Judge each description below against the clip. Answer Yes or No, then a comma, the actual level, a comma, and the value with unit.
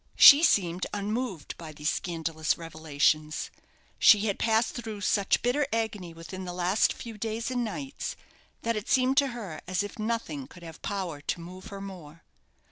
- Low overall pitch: No, high, 195 Hz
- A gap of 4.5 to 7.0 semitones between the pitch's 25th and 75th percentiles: Yes, wide, 5.4 semitones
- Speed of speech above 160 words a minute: Yes, average, 170 wpm